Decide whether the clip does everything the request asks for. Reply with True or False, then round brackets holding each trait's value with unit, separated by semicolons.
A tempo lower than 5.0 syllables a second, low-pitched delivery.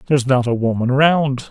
False (5.3 syllables/s; 130 Hz)